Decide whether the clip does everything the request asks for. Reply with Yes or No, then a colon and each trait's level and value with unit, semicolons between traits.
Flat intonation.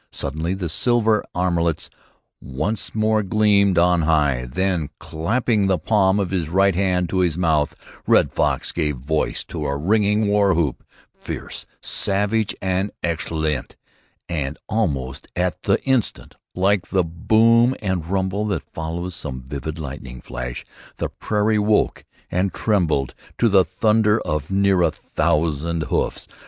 No: average, 4.7 semitones